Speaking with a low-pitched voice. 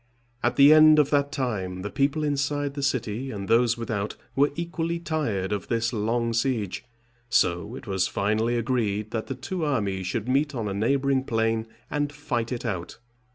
Yes: low, 120 Hz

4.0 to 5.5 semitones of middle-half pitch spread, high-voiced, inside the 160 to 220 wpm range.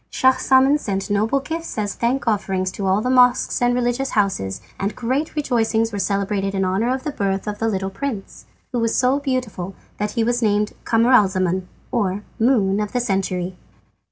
Yes: average, 4.4 semitones; high, 220 Hz; average, 180 wpm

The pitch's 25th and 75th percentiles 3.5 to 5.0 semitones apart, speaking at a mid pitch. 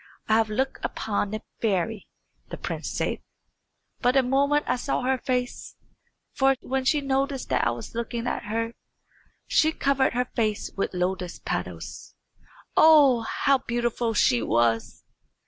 No: average, 4.0 semitones; high, 240 Hz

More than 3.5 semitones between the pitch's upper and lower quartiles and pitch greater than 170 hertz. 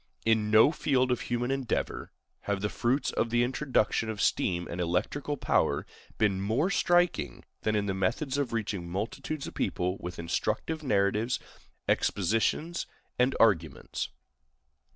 No: average, 5.2 semitones; low, 110 Hz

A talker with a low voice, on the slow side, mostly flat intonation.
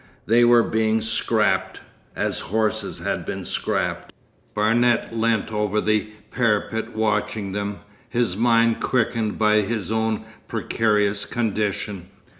Yes: low, 110 Hz; slow, 110 wpm; narrow, 1.5 semitones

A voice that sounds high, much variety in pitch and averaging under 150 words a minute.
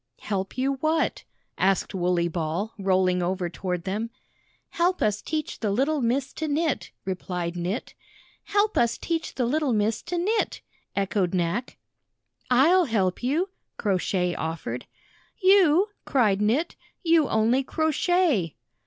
Yes: high, 225 Hz; wide, 9.0 semitones; slow, 135 wpm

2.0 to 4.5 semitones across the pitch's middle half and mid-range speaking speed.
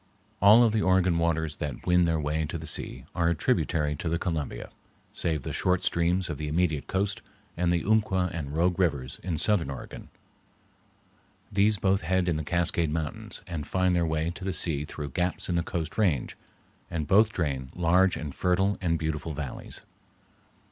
Yes: average, 3.1 semitones; average, 185 wpm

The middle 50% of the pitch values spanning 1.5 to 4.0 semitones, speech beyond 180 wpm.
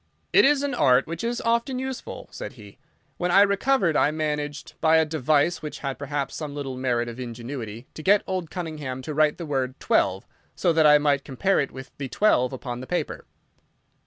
No: average, 5.1 semitones; average, 200 wpm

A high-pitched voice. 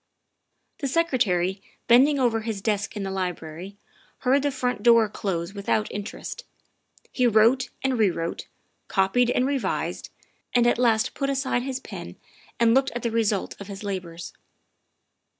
Yes: high, 225 Hz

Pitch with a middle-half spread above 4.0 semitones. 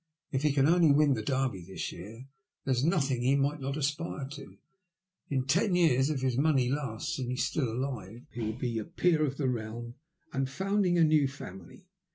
No: average, 3.7 semitones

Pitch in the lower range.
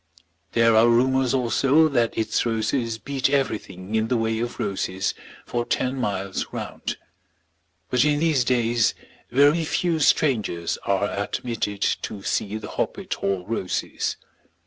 Yes: low, 120 Hz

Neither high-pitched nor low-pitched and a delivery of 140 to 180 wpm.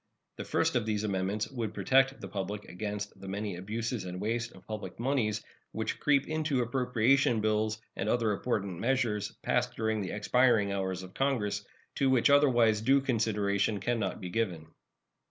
No: low, 110 Hz; average, 170 wpm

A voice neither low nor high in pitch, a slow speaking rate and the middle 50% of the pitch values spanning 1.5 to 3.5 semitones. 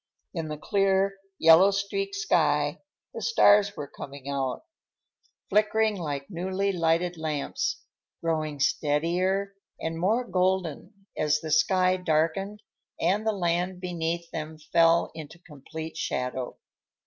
No: medium, 170 Hz; slow, 120 wpm; average, 3.9 semitones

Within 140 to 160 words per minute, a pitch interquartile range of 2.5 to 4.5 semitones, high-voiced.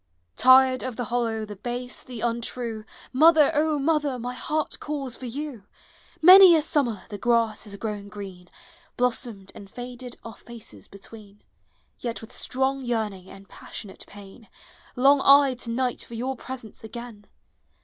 Yes: average, 150 wpm; average, 3.5 semitones; high, 240 Hz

